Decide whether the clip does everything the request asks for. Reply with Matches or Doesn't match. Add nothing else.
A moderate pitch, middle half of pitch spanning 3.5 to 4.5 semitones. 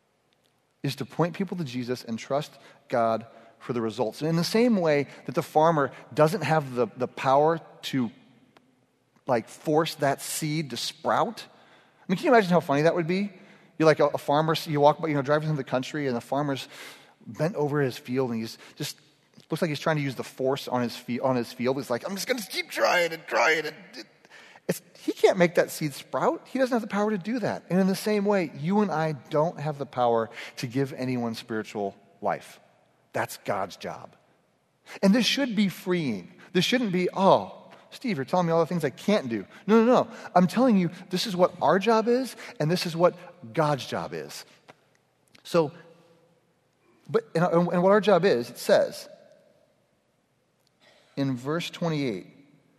Doesn't match